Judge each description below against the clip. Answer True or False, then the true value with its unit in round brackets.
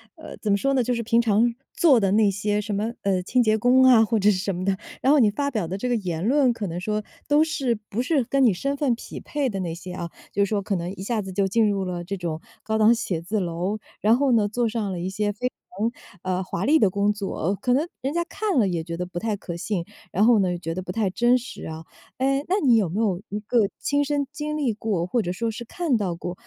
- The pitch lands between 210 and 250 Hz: True (215 Hz)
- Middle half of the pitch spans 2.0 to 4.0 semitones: False (4.8 semitones)